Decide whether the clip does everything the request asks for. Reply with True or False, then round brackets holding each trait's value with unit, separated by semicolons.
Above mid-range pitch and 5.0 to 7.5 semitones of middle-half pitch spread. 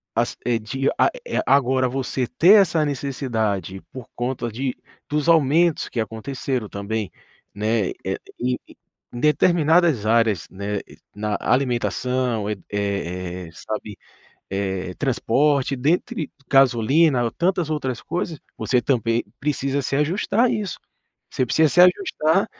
False (130 Hz; 5.5 semitones)